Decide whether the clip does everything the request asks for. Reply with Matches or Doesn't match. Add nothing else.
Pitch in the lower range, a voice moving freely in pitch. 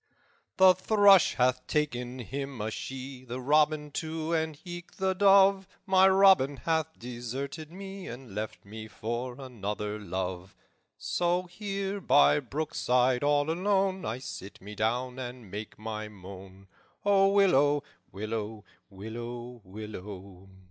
Matches